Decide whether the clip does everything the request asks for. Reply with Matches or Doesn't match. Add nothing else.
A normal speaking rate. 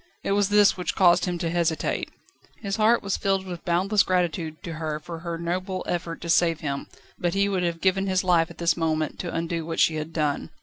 Doesn't match